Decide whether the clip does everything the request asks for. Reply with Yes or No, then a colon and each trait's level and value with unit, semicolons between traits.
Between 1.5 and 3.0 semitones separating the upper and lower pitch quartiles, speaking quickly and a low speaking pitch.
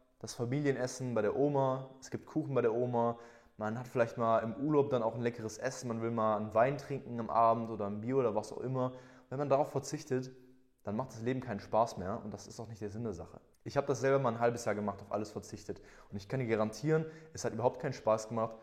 Yes: average, 2.7 semitones; fast, 260 wpm; low, 120 Hz